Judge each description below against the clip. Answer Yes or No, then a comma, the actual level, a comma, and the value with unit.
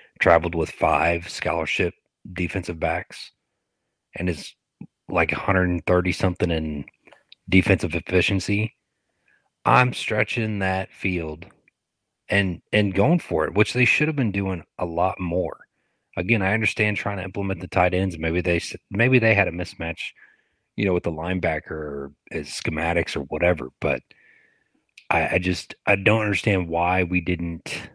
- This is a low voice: Yes, very low, 90 Hz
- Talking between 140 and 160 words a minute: Yes, average, 145 wpm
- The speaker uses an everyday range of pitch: Yes, average, 3.0 semitones